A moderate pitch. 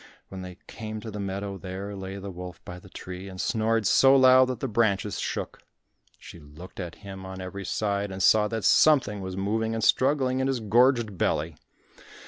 No: low, 100 Hz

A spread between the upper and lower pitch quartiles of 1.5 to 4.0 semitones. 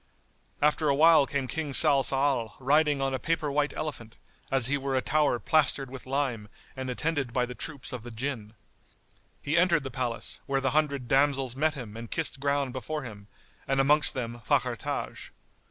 Yes: average, 2.8 semitones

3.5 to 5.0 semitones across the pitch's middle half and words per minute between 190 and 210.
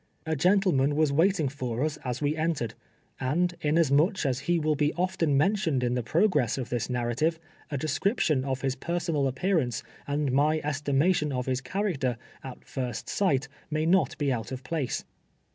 No: average, 4.1 semitones; average, 175 wpm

